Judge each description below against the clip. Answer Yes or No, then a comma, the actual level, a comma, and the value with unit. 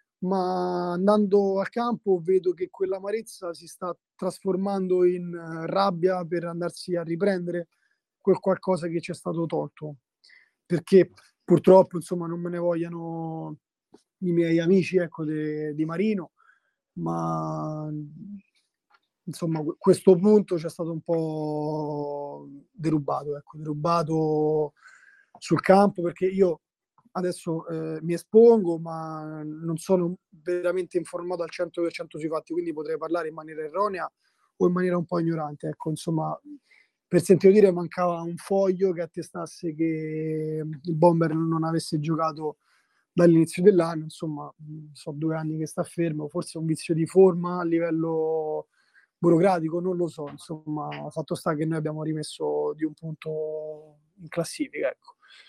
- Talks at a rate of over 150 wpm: No, average, 140 wpm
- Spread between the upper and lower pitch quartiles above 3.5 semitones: No, narrow, 2.6 semitones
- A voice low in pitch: No, medium, 170 Hz